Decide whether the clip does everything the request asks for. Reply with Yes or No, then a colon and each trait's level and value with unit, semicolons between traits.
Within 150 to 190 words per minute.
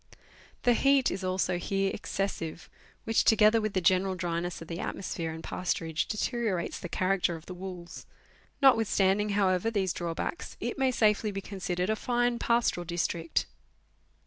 Yes: average, 155 wpm